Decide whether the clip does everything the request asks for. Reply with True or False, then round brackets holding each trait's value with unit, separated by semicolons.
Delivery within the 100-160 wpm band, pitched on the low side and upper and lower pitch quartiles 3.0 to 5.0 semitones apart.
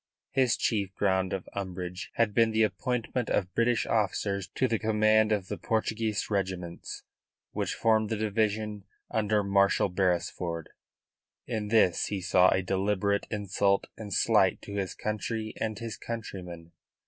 False (145 wpm; 105 Hz; 2.6 semitones)